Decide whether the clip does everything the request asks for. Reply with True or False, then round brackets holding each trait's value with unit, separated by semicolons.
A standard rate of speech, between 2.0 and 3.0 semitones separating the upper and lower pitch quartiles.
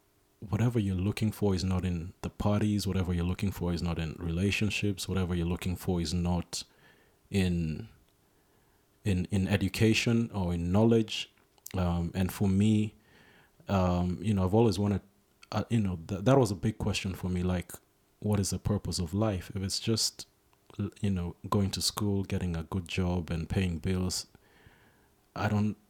True (175 wpm; 2.7 semitones)